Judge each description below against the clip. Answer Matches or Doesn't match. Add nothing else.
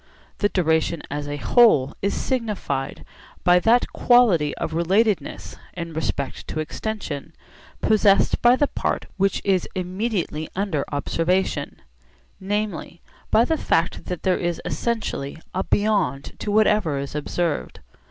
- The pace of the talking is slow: Matches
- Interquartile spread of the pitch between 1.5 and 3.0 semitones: Doesn't match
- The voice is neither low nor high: Matches